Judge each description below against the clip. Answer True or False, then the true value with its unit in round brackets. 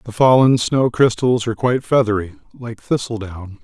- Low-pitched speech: True (115 Hz)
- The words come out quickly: False (150 wpm)